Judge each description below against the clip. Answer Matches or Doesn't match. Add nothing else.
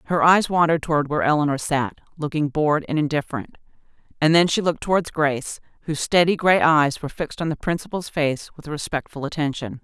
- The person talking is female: Matches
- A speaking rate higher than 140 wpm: Matches